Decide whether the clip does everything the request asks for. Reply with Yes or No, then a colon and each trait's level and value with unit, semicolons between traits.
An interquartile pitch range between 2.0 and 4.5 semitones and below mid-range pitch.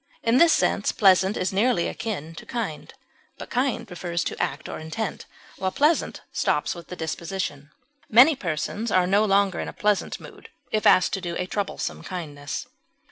No: average, 4.1 semitones; high, 190 Hz